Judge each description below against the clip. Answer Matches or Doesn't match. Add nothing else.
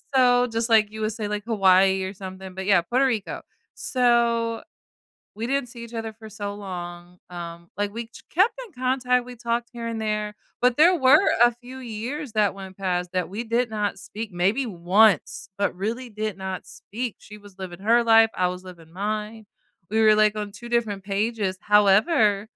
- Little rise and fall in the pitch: Doesn't match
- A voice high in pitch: Matches